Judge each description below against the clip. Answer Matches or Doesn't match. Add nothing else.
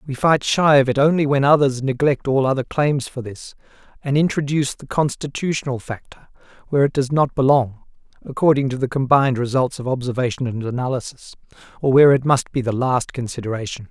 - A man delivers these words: Matches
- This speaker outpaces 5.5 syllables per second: Matches